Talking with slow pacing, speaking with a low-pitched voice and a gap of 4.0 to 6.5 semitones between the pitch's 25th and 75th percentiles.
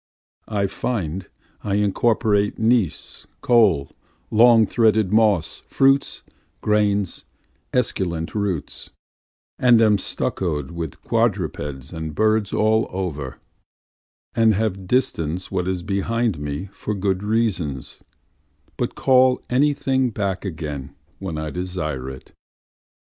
Yes: slow, 110 wpm; low, 100 Hz; average, 5.1 semitones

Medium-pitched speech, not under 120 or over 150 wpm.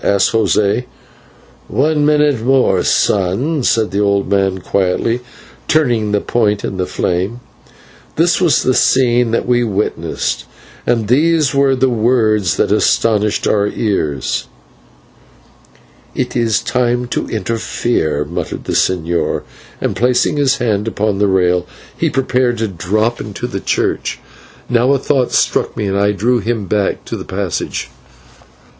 No: low, 110 Hz; average, 140 wpm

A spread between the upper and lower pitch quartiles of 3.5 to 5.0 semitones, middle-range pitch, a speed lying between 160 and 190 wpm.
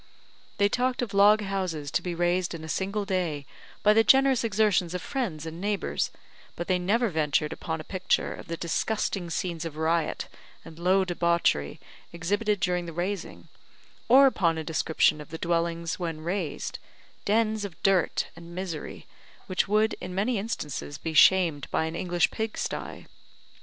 Yes: average, 3.8 semitones; medium, 180 Hz; average, 170 wpm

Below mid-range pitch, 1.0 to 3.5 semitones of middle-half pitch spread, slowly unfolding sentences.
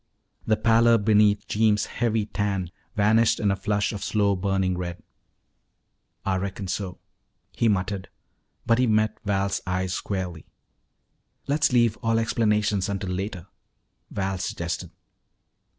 Yes: low, 100 Hz; narrow, 2.5 semitones; slow, 125 wpm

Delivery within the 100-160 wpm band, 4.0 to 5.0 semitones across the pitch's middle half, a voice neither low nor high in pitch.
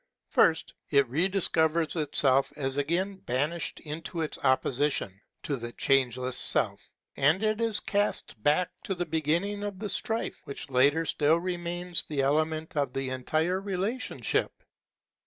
Yes: average, 140 wpm; average, 4.7 semitones; medium, 155 Hz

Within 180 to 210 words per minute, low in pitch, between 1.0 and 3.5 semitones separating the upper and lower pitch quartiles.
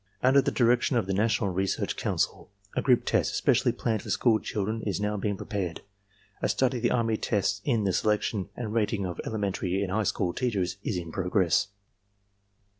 Yes: average, 190 wpm; low, 105 Hz; average, 3.1 semitones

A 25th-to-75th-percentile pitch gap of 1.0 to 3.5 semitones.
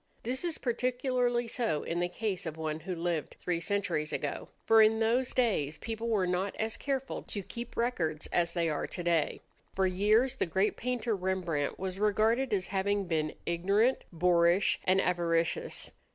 No: average, 5.1 semitones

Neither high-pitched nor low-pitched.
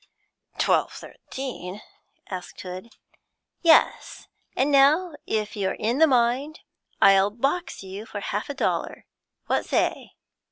No: high, 235 Hz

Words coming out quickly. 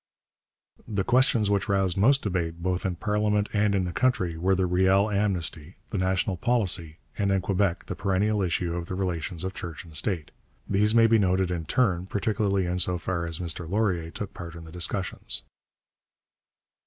No: average, 180 wpm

